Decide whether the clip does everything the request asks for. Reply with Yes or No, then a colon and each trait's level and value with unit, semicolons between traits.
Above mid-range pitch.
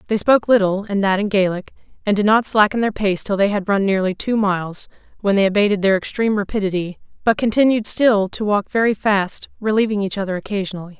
Yes: high, 205 Hz